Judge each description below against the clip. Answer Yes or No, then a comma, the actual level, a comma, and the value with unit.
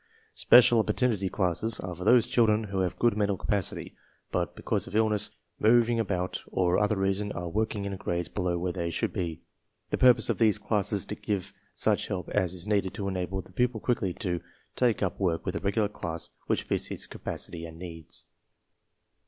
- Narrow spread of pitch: No, average, 3.2 semitones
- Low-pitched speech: Yes, low, 100 Hz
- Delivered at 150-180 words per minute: No, average, 195 wpm